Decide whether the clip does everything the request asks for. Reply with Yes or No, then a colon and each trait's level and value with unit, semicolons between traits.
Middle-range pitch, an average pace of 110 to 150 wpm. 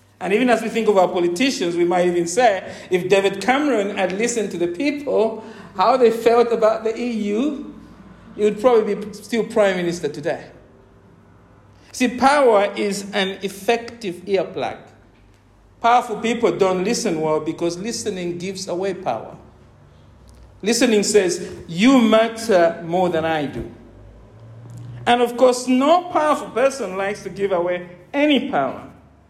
No: high, 200 Hz; average, 145 wpm